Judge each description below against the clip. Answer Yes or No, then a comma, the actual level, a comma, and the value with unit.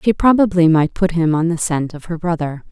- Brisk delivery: Yes, fast, 245 wpm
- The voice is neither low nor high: Yes, medium, 170 Hz